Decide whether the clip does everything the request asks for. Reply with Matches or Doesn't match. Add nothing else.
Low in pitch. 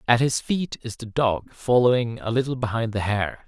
Matches